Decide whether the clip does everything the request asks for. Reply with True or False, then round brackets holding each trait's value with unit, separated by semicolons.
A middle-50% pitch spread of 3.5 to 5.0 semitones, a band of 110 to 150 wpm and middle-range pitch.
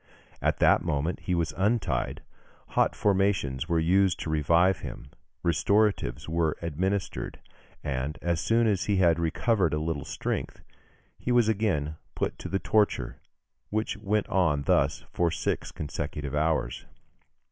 False (4.7 semitones; 145 wpm; 85 Hz)